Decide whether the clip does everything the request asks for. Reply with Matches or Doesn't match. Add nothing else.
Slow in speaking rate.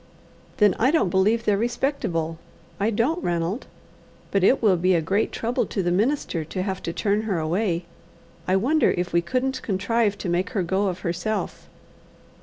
Doesn't match